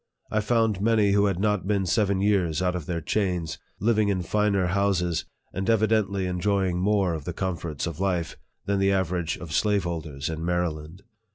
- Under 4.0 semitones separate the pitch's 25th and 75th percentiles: Yes, average, 2.8 semitones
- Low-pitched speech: Yes, very low, 95 Hz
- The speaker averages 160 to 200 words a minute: Yes, average, 175 wpm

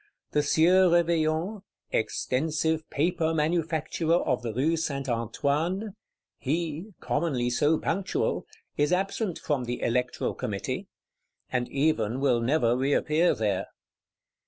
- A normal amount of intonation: Yes, average, 4.7 semitones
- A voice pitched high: No, medium, 155 Hz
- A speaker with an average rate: No, slow, 110 wpm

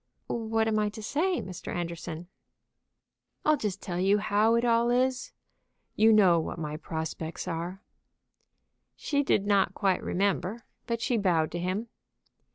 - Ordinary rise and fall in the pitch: Yes, average, 4.5 semitones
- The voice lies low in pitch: No, high, 205 Hz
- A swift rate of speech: No, average, 150 wpm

